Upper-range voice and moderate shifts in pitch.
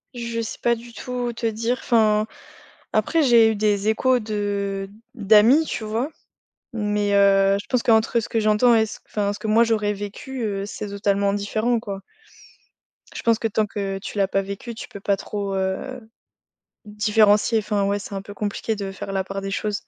No: high, 210 Hz; narrow, 2.3 semitones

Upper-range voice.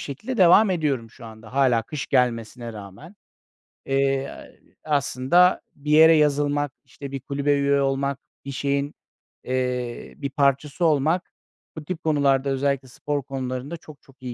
No: medium, 140 Hz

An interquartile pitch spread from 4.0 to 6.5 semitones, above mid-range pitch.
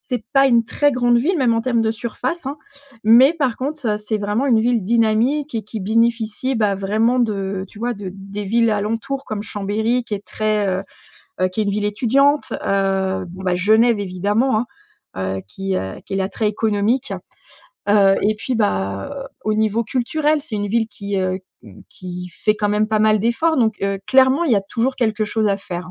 No: average, 3.3 semitones; high, 215 Hz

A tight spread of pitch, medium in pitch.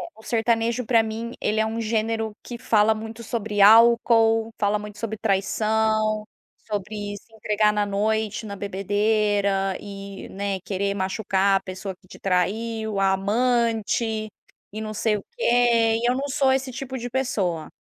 No: narrow, 2.0 semitones; high, 215 Hz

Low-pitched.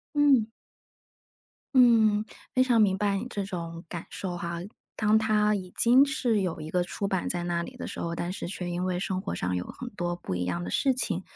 No: high, 190 Hz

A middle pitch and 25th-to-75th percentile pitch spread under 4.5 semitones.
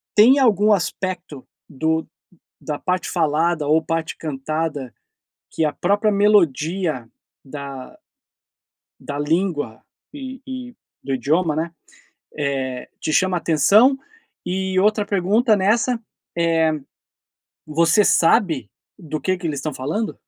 No: medium, 165 Hz; average, 5.2 semitones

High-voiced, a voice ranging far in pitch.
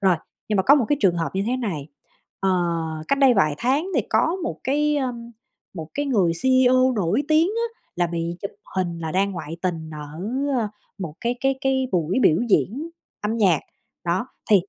Yes: high, 205 Hz; wide, 7.5 semitones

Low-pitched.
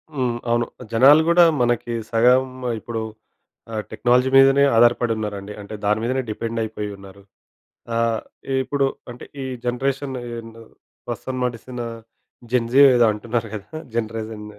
Yes: low, 120 Hz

